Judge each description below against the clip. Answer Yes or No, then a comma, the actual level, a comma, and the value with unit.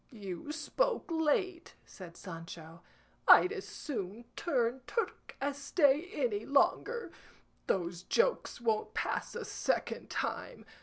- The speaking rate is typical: No, slow, 115 wpm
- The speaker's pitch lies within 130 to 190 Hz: No, very high, 280 Hz